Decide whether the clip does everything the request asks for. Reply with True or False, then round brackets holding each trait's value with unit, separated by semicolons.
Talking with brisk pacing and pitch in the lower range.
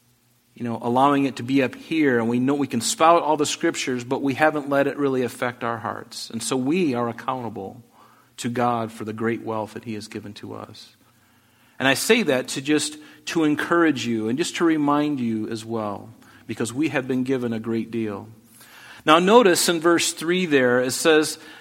True (210 wpm; 125 Hz)